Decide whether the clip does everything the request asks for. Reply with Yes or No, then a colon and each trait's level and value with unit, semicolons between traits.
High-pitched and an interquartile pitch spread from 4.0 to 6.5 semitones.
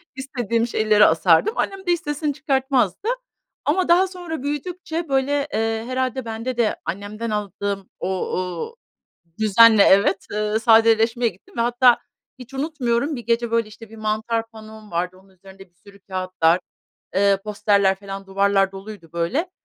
Yes: high, 225 Hz; average, 4.8 semitones